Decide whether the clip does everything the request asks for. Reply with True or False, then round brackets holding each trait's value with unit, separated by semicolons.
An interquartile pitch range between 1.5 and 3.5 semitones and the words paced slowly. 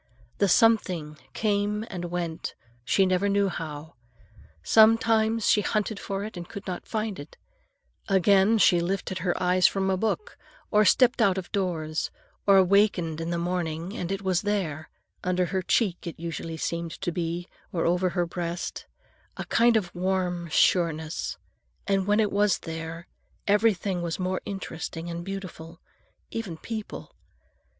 False (3.0 semitones; 150 wpm)